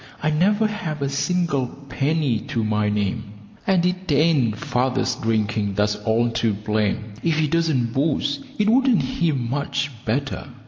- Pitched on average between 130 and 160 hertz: Yes, medium, 140 Hz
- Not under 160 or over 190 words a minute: No, average, 150 wpm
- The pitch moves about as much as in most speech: No, wide, 6.7 semitones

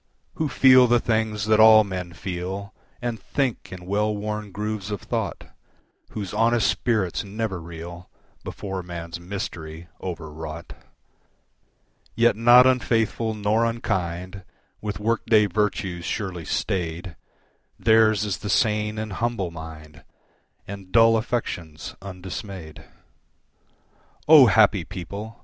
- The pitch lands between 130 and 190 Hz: No, low, 100 Hz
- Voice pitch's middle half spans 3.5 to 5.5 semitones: Yes, average, 3.8 semitones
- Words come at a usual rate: No, slow, 120 wpm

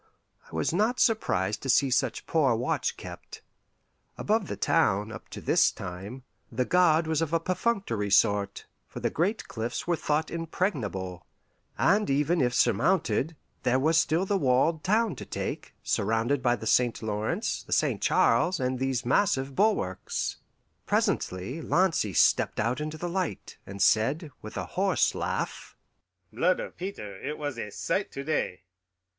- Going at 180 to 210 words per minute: No, average, 160 wpm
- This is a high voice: No, medium, 140 Hz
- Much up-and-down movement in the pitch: Yes, wide, 7.4 semitones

